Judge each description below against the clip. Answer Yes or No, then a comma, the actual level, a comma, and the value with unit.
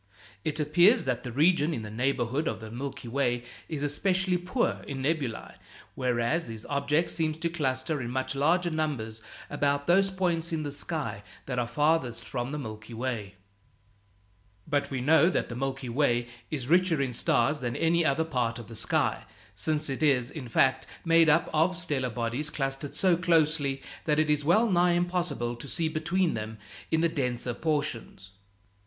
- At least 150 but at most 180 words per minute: Yes, average, 175 wpm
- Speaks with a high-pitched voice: No, medium, 145 Hz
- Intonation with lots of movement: No, average, 4.7 semitones